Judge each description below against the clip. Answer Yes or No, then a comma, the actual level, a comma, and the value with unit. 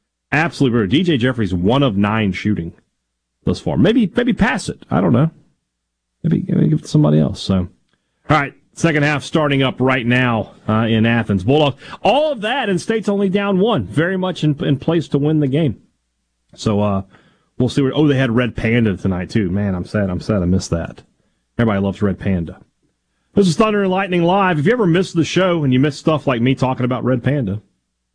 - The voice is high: No, low, 130 Hz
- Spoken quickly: Yes, fast, 215 wpm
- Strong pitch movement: Yes, wide, 8.5 semitones